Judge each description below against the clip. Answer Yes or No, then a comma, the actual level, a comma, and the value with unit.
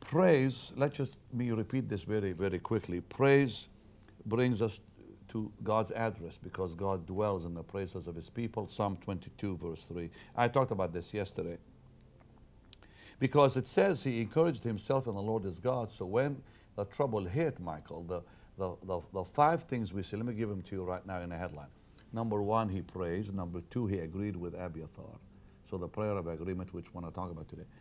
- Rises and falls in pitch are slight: No, average, 4.3 semitones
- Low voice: Yes, low, 105 Hz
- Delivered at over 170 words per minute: Yes, average, 195 wpm